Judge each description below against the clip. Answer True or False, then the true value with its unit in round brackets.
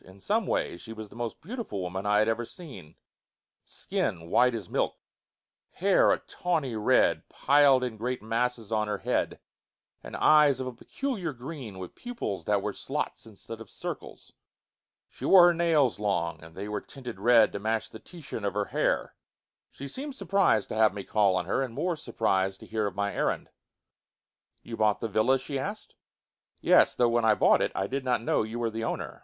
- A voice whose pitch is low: True (115 Hz)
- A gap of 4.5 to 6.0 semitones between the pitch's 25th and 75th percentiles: True (5.1 semitones)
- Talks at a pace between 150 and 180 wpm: False (200 wpm)